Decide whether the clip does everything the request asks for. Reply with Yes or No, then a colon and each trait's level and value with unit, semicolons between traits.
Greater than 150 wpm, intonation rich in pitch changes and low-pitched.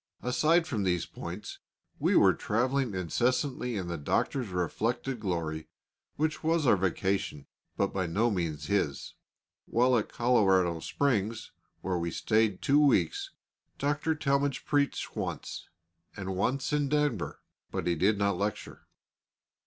No: slow, 135 wpm; wide, 6.9 semitones; low, 110 Hz